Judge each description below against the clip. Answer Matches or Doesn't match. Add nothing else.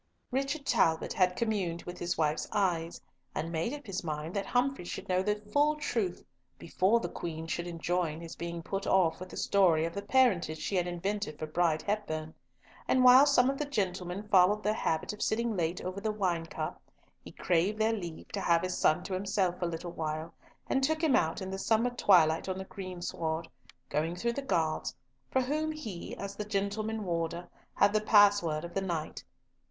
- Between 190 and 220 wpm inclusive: Matches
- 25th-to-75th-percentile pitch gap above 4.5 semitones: Doesn't match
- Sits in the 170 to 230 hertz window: Matches